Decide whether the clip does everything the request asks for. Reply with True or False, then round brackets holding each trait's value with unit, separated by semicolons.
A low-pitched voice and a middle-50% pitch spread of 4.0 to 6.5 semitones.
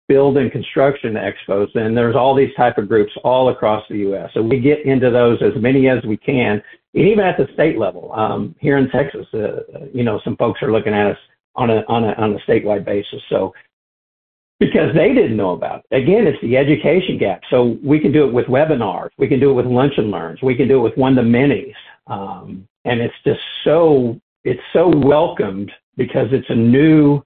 True (125 Hz; 4.3 semitones)